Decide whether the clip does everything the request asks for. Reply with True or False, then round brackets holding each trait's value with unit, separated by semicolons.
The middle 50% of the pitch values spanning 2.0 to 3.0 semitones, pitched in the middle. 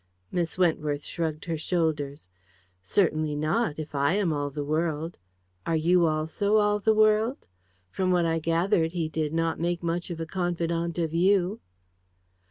True (2.5 semitones; 165 Hz)